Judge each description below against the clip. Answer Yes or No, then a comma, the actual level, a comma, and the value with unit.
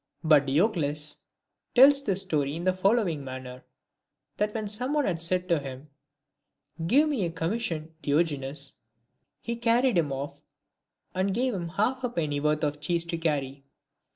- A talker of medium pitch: Yes, medium, 170 Hz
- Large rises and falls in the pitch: Yes, wide, 6.6 semitones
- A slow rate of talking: No, average, 155 wpm